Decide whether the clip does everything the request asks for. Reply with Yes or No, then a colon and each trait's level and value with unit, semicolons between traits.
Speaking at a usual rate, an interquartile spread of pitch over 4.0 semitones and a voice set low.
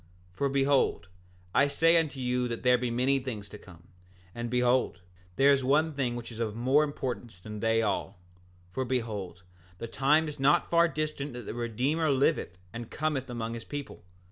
No: average, 180 wpm; average, 3.7 semitones; low, 125 Hz